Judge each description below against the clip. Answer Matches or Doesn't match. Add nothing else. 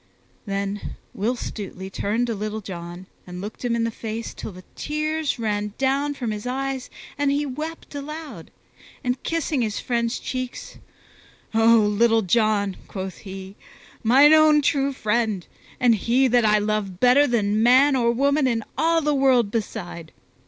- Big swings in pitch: Doesn't match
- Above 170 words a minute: Doesn't match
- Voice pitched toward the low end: Doesn't match